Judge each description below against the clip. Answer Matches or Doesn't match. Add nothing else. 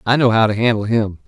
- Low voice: Matches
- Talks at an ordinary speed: Doesn't match